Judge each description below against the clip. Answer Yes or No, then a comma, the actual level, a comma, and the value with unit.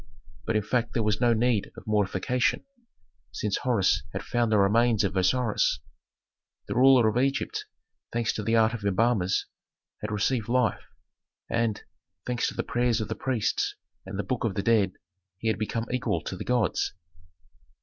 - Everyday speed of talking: Yes, average, 170 wpm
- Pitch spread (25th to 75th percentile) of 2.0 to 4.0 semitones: Yes, average, 2.8 semitones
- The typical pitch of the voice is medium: No, low, 110 Hz